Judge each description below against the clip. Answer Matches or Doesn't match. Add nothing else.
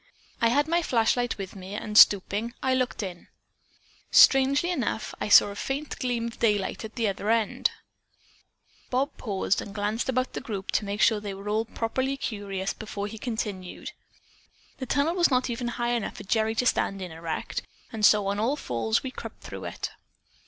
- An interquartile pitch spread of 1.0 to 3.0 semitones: Doesn't match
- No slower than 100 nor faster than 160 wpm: Doesn't match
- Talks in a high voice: Matches